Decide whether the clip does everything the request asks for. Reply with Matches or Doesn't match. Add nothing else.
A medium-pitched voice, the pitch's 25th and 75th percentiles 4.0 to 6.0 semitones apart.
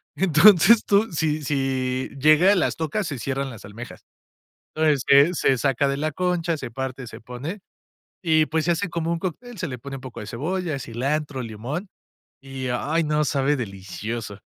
Matches